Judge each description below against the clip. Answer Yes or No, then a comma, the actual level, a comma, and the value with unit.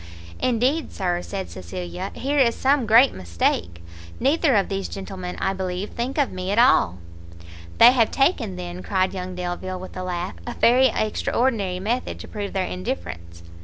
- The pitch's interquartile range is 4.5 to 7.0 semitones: Yes, average, 5.2 semitones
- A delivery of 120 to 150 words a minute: No, average, 165 wpm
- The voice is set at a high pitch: Yes, high, 195 Hz